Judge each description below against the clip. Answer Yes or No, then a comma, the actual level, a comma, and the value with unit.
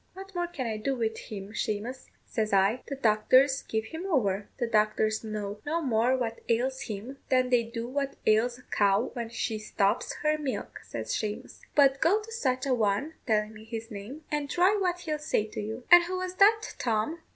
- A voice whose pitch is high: Yes, high, 245 Hz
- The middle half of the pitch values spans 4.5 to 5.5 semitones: Yes, average, 5.1 semitones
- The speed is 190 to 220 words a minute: Yes, fast, 205 wpm